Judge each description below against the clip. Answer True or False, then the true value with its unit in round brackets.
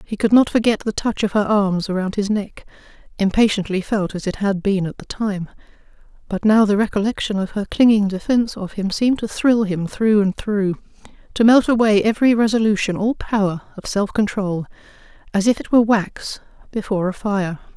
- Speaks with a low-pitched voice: False (205 Hz)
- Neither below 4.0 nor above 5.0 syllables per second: False (5.4 syllables/s)